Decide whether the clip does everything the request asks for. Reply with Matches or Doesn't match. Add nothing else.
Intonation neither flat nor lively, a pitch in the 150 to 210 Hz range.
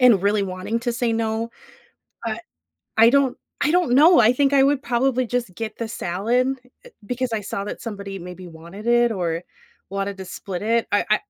Doesn't match